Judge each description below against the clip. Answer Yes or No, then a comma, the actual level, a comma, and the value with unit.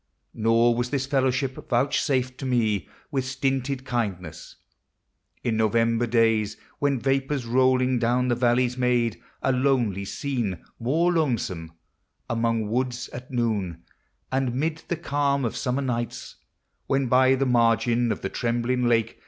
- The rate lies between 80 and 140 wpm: Yes, slow, 135 wpm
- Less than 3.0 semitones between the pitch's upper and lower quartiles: Yes, narrow, 2.4 semitones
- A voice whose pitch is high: No, low, 125 Hz